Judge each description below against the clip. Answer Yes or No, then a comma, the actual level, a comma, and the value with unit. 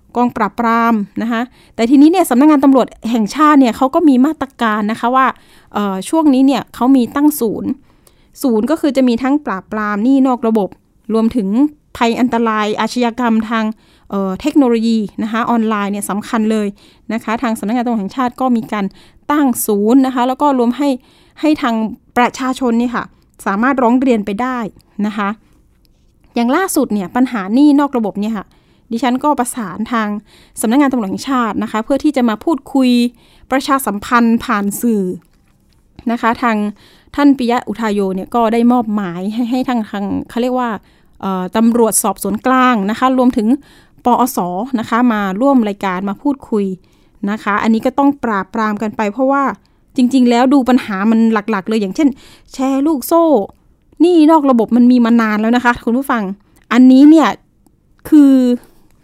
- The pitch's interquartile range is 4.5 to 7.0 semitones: No, average, 3.3 semitones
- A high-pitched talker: Yes, high, 235 Hz